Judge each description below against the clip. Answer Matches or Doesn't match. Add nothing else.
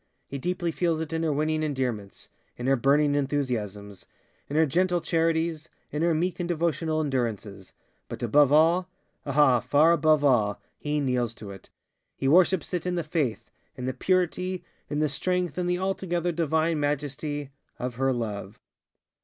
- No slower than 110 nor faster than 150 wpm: Matches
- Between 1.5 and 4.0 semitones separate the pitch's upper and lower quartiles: Doesn't match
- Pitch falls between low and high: Matches